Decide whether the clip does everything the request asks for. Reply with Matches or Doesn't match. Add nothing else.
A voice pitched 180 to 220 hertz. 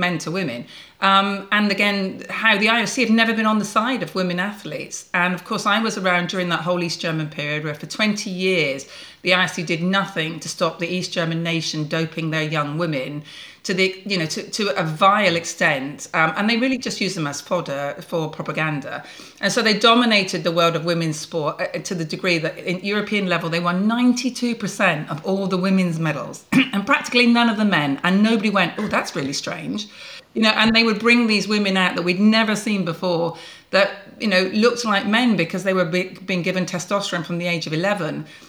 Matches